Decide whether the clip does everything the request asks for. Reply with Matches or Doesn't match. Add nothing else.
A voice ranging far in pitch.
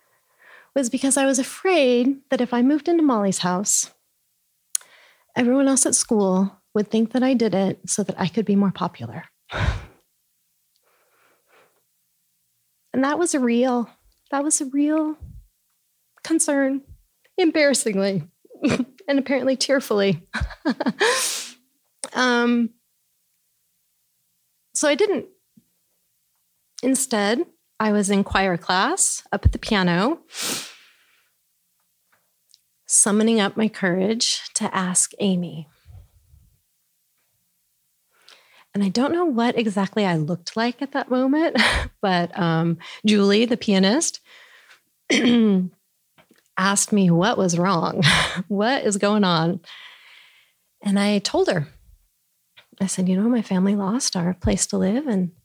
Matches